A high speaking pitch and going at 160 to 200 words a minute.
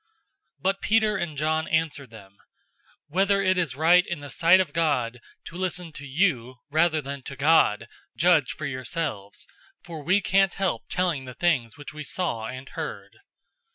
No: medium, 160 Hz; average, 175 wpm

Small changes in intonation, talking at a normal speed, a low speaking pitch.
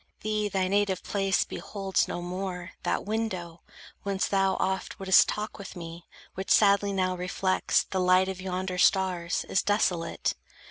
No: narrow, 1.5 semitones; average, 150 wpm; high, 190 Hz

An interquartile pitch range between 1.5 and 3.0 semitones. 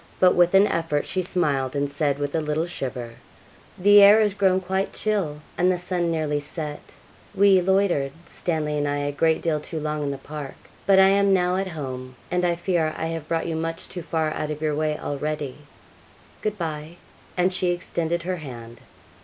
No: average, 3.6 semitones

